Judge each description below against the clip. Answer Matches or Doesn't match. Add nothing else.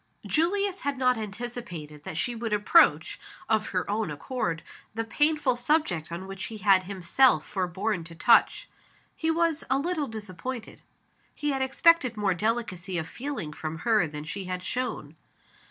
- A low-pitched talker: Doesn't match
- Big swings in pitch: Matches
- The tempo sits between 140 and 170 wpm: Matches